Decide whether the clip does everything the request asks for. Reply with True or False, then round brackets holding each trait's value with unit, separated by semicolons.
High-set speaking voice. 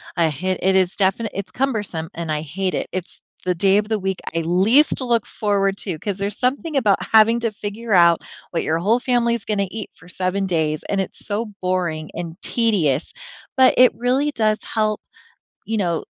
True (200 Hz)